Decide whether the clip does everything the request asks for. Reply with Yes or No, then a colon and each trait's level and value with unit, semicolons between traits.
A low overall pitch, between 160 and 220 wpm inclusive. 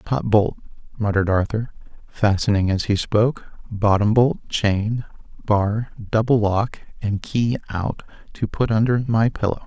No: low, 105 Hz; slow, 135 wpm